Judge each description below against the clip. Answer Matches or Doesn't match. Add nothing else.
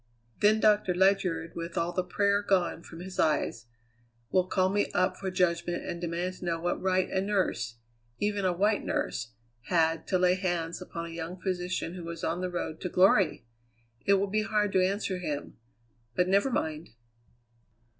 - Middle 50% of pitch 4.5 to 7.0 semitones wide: Doesn't match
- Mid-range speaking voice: Matches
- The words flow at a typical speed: Matches